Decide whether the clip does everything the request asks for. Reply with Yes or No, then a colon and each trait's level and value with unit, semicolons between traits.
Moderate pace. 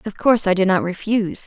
No: fast, 245 wpm